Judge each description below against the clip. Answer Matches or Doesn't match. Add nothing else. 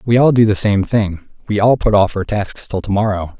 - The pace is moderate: Doesn't match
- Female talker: Doesn't match